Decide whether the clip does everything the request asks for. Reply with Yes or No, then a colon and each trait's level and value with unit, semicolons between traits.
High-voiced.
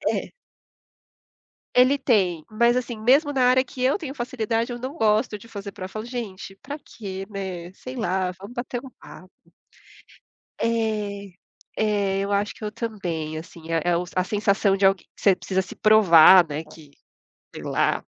Yes: high, 210 Hz